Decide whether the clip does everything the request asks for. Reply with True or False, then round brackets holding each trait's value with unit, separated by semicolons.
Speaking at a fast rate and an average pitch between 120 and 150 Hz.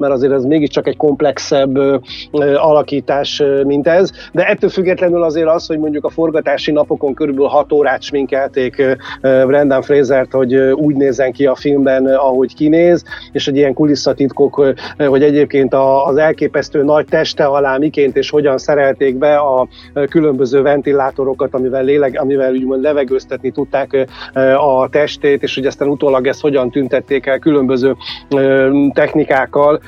True (160 wpm; 140 Hz)